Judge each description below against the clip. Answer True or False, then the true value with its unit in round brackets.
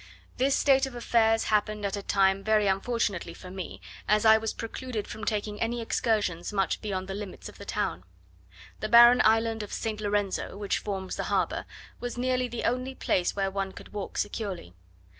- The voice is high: True (215 Hz)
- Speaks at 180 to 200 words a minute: True (185 wpm)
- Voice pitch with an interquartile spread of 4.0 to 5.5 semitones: False (2.9 semitones)